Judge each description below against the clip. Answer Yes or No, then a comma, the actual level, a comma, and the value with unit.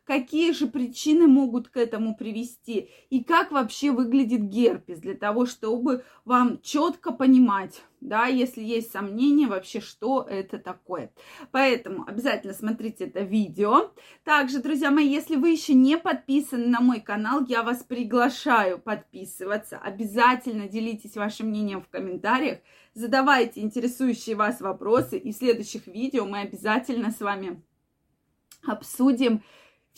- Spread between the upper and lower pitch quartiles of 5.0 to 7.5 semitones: No, average, 3.9 semitones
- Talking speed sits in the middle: Yes, average, 130 wpm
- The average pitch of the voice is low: No, high, 240 Hz